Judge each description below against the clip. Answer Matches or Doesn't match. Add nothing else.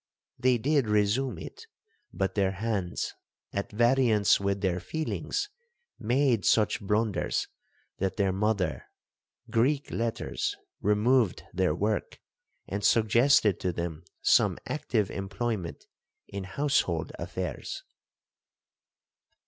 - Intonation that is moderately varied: Matches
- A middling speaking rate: Doesn't match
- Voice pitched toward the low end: Matches